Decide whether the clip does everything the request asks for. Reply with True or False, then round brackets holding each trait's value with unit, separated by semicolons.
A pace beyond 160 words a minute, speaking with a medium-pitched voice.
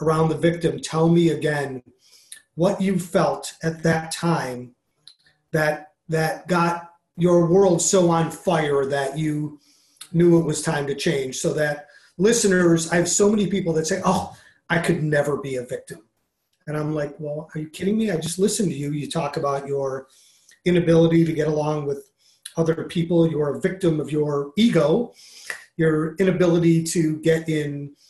True (170 wpm; 160 Hz)